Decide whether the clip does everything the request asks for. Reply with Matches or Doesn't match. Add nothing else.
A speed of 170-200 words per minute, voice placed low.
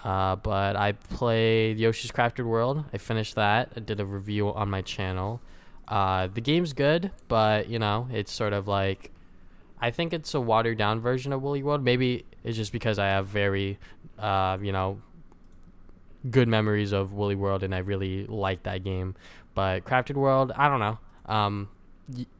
Matches